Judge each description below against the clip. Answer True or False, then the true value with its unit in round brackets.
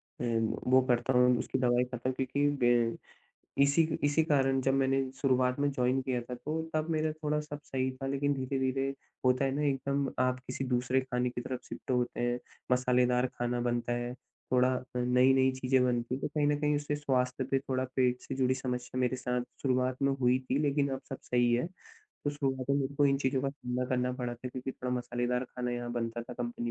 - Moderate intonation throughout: False (1.7 semitones)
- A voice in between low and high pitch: False (130 Hz)